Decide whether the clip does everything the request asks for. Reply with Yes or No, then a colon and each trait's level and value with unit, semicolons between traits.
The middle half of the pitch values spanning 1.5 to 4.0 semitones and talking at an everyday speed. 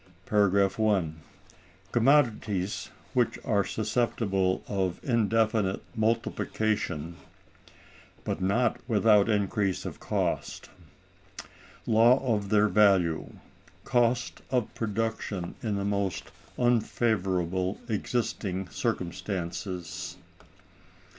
No: average, 3.2 semitones; slow, 80 wpm